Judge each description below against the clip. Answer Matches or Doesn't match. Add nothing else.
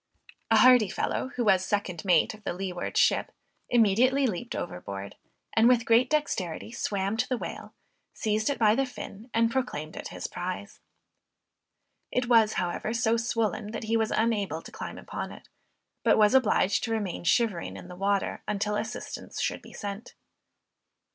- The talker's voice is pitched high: Matches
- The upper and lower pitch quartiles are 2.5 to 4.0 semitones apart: Matches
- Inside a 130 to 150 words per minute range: Doesn't match